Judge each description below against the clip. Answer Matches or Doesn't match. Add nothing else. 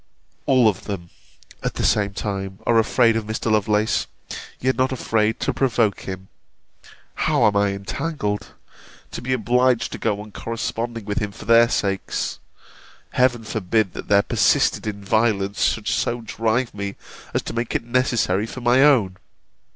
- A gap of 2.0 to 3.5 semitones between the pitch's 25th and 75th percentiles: Matches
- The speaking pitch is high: Doesn't match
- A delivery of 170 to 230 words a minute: Doesn't match